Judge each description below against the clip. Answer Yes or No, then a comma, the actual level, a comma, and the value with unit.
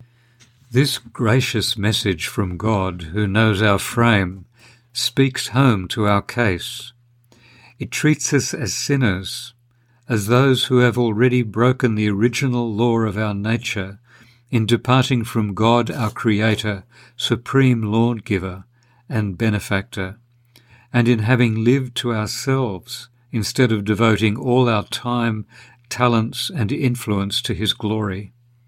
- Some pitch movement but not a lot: No, narrow, 2.3 semitones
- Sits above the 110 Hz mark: Yes, low, 120 Hz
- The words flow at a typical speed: No, slow, 125 wpm